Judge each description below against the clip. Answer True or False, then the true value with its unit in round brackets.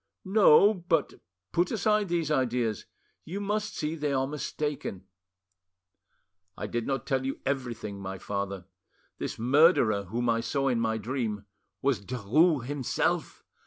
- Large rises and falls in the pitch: True (5.9 semitones)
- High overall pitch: False (130 Hz)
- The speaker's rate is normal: False (125 wpm)